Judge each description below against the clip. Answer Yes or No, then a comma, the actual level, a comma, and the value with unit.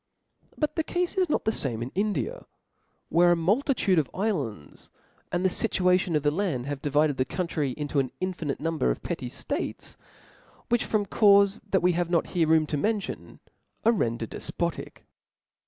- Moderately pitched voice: Yes, medium, 175 Hz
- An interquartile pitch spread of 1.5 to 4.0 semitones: No, wide, 5.6 semitones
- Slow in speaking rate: No, average, 170 wpm